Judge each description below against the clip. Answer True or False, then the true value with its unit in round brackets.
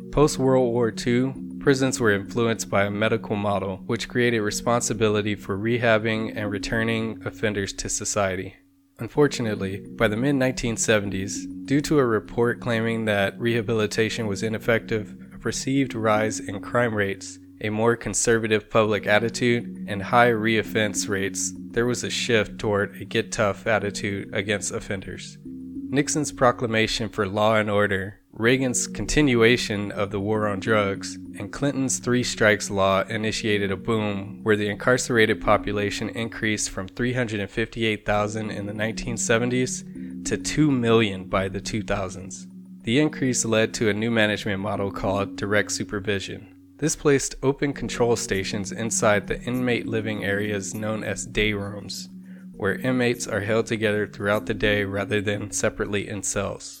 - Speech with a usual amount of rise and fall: True (3.0 semitones)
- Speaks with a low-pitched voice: True (105 Hz)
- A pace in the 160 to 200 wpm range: False (140 wpm)